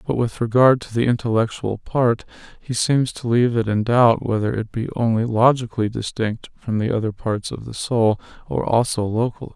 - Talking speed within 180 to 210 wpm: Yes, average, 190 wpm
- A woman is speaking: No, male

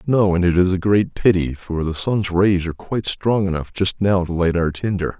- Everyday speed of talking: No, fast, 245 wpm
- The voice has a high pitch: No, very low, 95 Hz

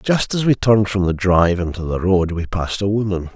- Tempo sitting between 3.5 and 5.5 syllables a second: No, 5.8 syllables/s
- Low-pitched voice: Yes, very low, 95 Hz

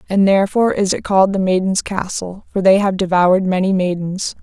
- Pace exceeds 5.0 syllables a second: Yes, 5.8 syllables/s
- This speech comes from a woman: Yes, female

